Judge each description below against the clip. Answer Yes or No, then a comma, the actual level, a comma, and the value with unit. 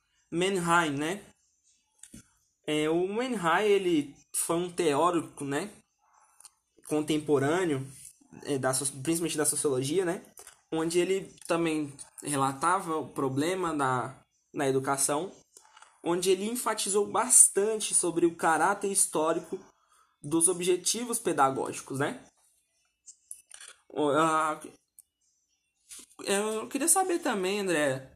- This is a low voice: No, medium, 165 Hz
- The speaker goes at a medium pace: No, slow, 95 wpm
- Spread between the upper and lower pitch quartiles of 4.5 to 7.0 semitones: Yes, average, 5.2 semitones